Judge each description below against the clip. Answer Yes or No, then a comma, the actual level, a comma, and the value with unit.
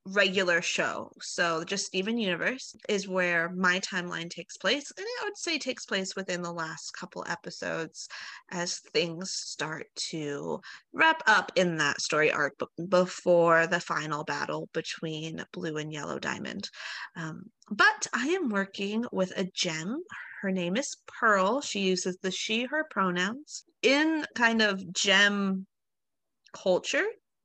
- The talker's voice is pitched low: No, high, 190 Hz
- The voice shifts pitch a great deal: Yes, wide, 5.7 semitones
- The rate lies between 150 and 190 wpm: No, average, 140 wpm